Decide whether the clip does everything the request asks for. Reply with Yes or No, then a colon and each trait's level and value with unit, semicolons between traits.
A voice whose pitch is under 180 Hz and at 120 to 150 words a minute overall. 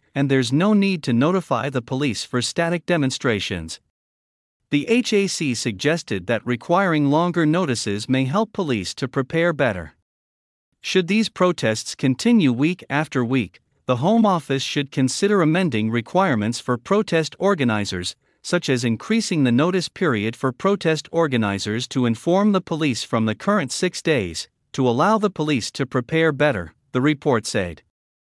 Yes: medium, 140 Hz; average, 145 wpm